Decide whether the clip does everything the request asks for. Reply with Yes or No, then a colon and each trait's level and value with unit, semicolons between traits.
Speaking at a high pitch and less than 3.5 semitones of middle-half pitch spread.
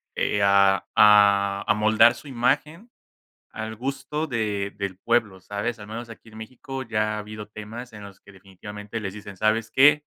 No: low, 110 Hz; average, 2.8 semitones